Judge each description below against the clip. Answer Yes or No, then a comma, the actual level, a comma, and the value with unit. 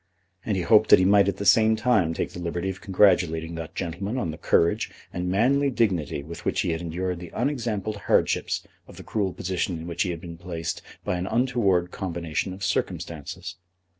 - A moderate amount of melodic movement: Yes, average, 3.8 semitones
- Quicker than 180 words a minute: Yes, average, 200 wpm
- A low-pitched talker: Yes, very low, 90 Hz